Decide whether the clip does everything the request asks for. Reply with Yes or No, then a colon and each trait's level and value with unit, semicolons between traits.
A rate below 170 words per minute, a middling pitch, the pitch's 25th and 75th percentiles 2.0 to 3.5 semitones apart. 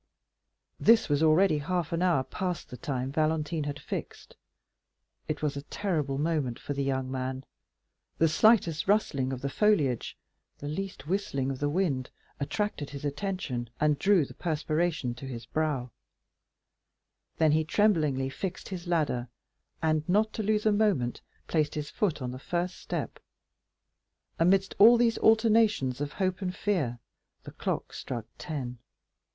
No: average, 150 wpm; medium, 155 Hz; wide, 5.6 semitones